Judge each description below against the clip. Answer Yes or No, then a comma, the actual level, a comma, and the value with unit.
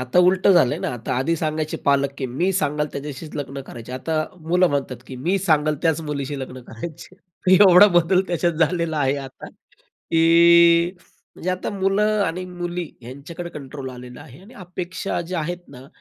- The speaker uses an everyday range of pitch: Yes, average, 4.3 semitones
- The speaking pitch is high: No, medium, 160 Hz